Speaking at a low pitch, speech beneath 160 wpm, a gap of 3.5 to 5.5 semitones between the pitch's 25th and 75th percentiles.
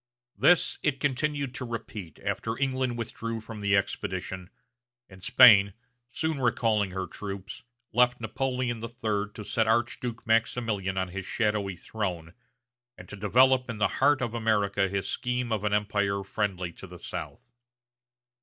Yes: low, 110 Hz; average, 150 wpm; average, 3.8 semitones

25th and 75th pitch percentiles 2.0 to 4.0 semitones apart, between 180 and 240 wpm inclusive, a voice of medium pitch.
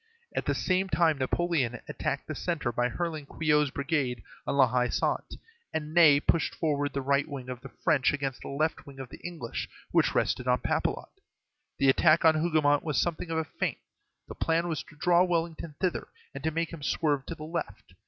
Yes: average, 3.4 semitones; average, 200 wpm; medium, 150 Hz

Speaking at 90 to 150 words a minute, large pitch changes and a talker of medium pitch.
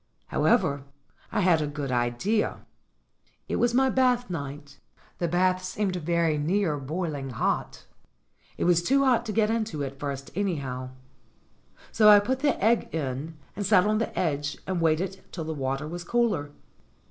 No: average, 165 wpm; wide, 6.4 semitones; medium, 175 Hz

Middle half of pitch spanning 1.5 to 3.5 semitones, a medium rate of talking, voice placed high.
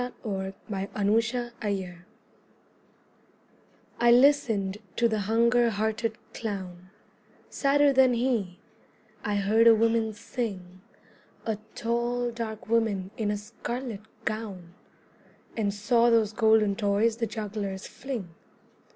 No: average, 2.7 semitones; slow, 110 wpm; high, 220 Hz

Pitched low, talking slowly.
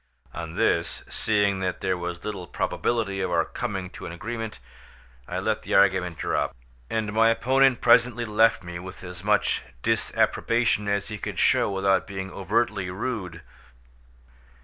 No: low, 100 Hz; average, 150 wpm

